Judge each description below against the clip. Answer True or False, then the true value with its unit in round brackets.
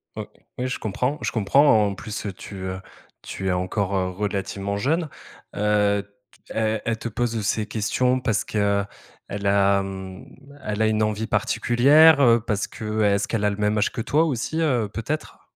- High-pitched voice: False (105 Hz)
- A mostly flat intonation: False (3.2 semitones)